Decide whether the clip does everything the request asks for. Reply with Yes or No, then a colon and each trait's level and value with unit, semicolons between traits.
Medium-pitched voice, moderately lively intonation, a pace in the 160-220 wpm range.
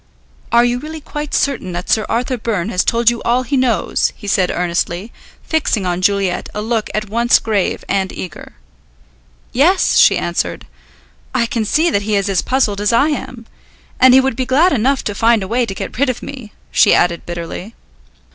No: high, 230 Hz; average, 4.5 semitones; average, 195 wpm